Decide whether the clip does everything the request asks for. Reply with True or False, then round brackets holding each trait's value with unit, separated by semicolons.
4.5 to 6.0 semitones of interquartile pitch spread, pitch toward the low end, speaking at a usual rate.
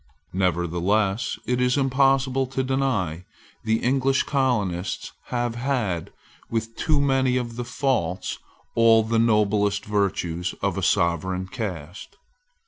False (5.6 semitones; 115 Hz; 125 wpm)